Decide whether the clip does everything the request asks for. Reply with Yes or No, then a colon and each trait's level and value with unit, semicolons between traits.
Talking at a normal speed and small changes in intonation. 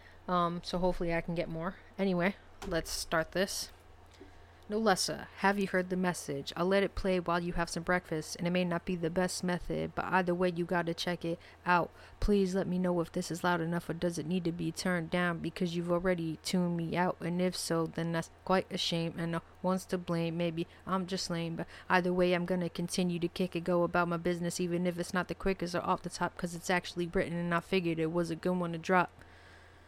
No: fast, 245 wpm; narrow, 1.4 semitones